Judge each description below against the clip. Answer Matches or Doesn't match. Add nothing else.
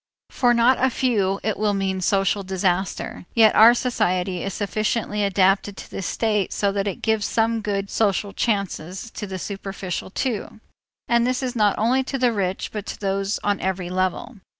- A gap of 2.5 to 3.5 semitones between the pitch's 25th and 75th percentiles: Matches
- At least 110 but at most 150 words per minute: Doesn't match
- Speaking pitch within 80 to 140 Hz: Doesn't match